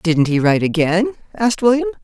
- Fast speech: No, average, 175 wpm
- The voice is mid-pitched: No, high, 200 Hz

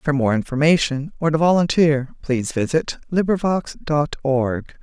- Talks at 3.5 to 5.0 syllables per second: Yes, 4.6 syllables/s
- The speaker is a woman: Yes, female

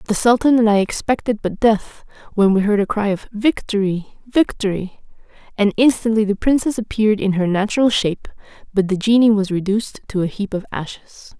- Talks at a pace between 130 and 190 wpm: Yes, average, 180 wpm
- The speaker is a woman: Yes, female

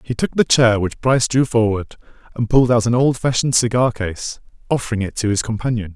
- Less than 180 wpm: No, average, 200 wpm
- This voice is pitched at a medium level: No, low, 115 Hz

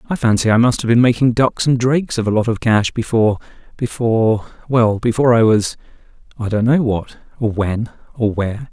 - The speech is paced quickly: No, average, 180 wpm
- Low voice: Yes, low, 115 Hz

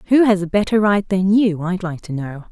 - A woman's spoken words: Yes, female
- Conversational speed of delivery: No, fast, 260 wpm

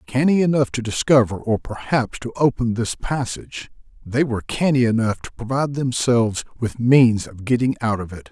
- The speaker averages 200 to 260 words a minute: No, average, 175 wpm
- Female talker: No, male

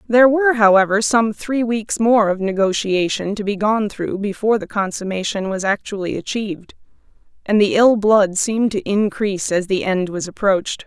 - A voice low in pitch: No, high, 205 Hz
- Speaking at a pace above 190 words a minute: No, average, 170 wpm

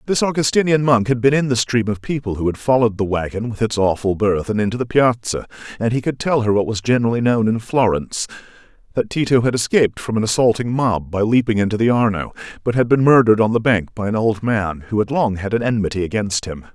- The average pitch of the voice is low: Yes, low, 115 Hz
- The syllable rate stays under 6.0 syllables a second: No, 6.3 syllables/s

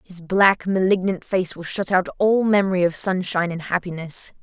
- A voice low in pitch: No, medium, 185 Hz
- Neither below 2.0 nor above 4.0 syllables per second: No, 5.1 syllables/s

